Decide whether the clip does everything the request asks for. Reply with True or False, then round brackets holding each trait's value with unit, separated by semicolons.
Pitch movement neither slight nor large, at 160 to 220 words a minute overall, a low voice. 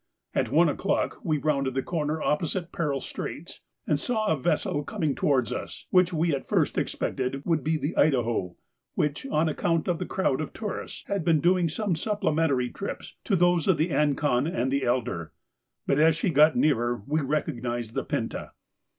False (3.8 semitones; 175 wpm; 150 Hz)